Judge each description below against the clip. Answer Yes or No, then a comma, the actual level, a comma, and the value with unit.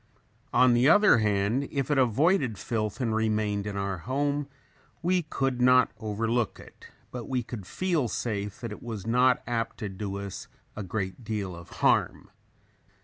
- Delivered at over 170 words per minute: No, average, 165 wpm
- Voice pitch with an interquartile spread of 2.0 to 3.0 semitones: No, average, 3.9 semitones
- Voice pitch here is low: Yes, low, 115 Hz